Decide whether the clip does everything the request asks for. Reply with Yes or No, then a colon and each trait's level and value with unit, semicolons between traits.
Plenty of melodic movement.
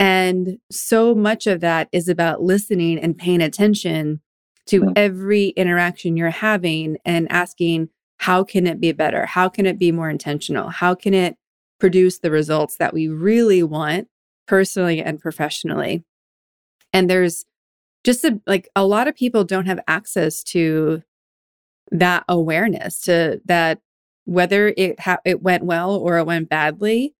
No: average, 2.9 semitones